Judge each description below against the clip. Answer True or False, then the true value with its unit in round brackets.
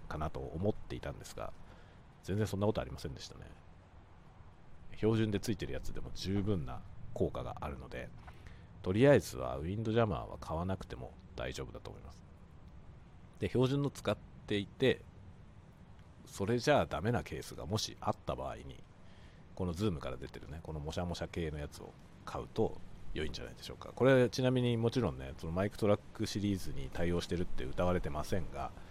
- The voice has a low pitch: True (90 Hz)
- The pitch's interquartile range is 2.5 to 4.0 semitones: False (4.7 semitones)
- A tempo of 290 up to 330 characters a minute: False (390 characters per minute)